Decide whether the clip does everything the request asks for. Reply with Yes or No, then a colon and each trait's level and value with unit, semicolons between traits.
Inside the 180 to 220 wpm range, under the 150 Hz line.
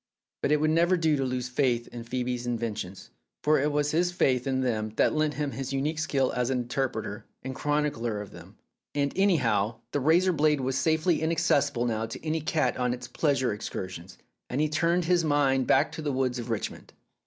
Yes: average, 200 wpm; low, 135 Hz